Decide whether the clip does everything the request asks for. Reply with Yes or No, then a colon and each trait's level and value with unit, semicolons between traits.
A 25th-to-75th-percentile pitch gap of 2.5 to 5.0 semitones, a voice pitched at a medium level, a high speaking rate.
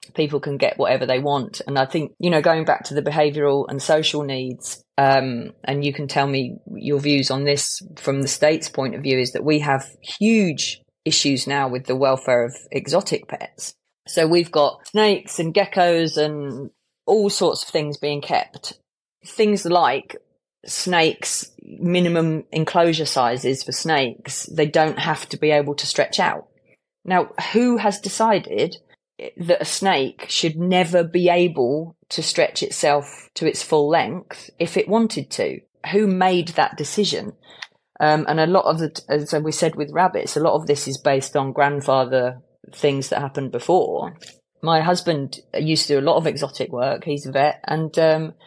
No: average, 3.9 semitones; medium, 150 Hz; average, 175 wpm